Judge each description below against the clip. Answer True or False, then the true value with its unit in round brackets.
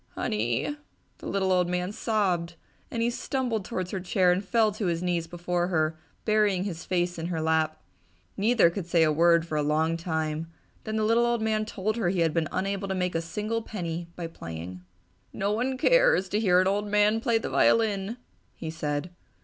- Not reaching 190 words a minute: False (200 wpm)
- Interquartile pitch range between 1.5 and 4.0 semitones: False (4.4 semitones)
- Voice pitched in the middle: True (180 Hz)